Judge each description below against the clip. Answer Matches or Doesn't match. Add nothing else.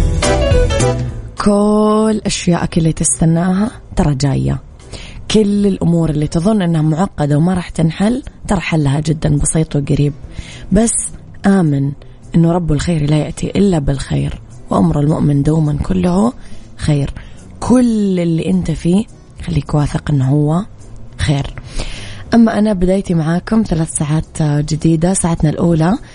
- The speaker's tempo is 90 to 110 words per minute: Doesn't match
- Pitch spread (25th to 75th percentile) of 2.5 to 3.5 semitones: Doesn't match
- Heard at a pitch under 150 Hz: Doesn't match